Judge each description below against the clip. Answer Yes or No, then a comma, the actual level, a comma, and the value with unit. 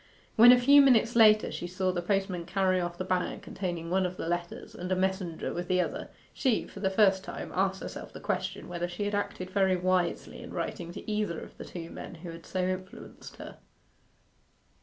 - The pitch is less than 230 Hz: Yes, medium, 185 Hz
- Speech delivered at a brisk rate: Yes, fast, 210 wpm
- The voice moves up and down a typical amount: No, narrow, 2.1 semitones